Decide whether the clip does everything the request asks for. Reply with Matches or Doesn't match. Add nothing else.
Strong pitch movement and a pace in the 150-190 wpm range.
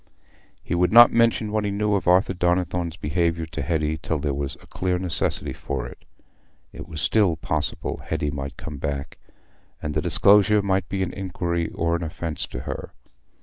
Doesn't match